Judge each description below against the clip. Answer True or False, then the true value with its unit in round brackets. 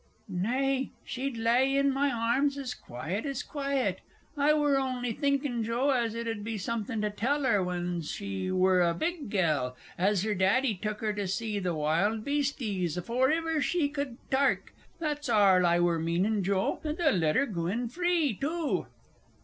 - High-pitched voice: True (230 Hz)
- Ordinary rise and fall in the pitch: False (6.7 semitones)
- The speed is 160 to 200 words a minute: True (180 wpm)